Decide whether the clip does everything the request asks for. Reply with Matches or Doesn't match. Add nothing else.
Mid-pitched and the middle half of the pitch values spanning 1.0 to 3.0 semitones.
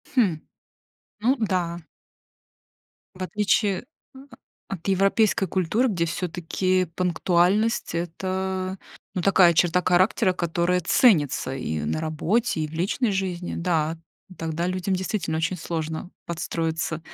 Matches